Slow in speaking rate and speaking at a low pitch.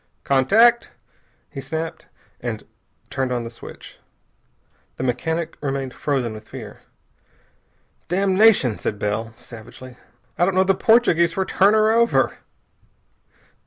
No: slow, 120 wpm; medium, 155 Hz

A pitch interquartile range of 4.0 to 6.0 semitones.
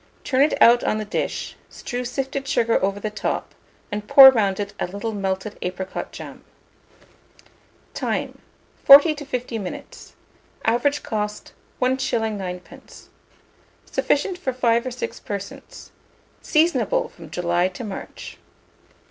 Yes: average, 4.9 semitones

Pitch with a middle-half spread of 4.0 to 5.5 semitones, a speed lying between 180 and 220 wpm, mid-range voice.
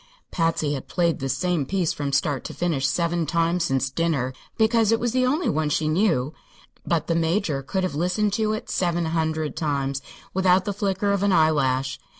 Yes: average, 4.6 semitones; average, 190 wpm; medium, 165 Hz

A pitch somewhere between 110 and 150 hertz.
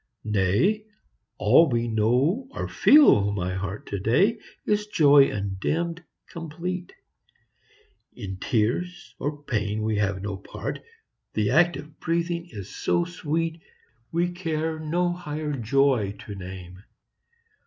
Yes: medium, 140 Hz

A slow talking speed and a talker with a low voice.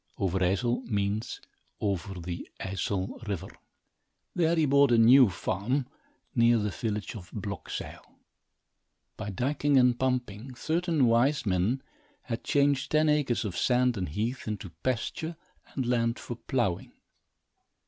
Yes: slow, 130 wpm; low, 120 Hz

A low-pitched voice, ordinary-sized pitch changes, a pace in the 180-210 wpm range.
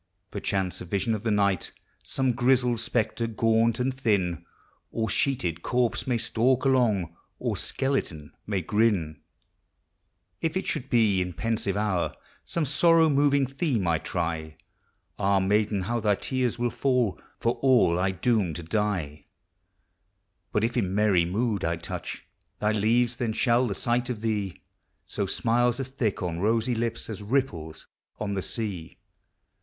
No: low, 110 Hz; average, 4.4 semitones; average, 150 wpm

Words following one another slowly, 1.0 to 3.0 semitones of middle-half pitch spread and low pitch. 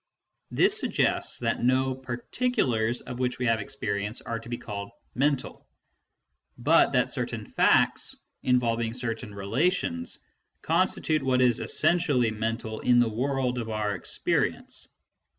Yes: slow, 130 wpm; average, 2.7 semitones; low, 120 Hz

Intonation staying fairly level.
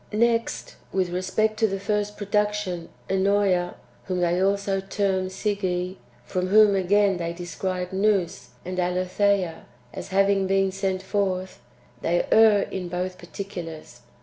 Yes: narrow, 1.9 semitones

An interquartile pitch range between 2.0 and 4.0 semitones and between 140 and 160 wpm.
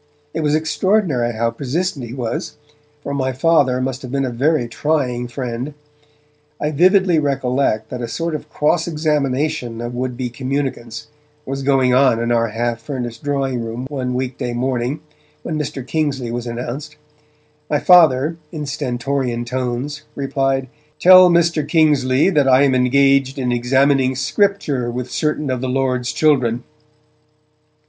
Yes: average, 3.4 semitones; average, 150 wpm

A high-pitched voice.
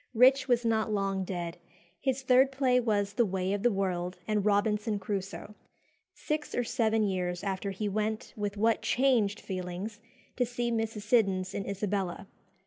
Yes: high, 210 Hz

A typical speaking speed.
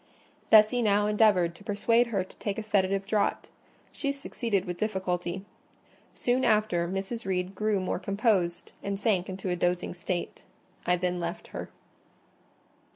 Yes: average, 150 wpm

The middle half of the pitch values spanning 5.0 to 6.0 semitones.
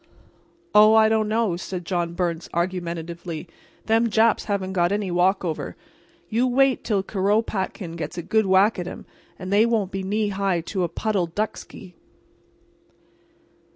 No: average, 3.6 semitones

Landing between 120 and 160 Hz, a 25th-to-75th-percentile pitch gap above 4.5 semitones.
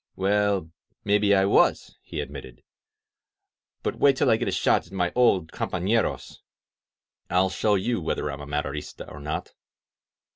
No: very low, 95 Hz; wide, 5.5 semitones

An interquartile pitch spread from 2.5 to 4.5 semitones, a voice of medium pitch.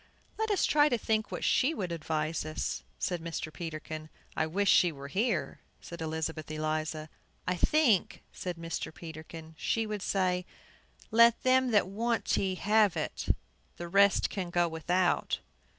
No: average, 5.1 semitones; medium, 175 Hz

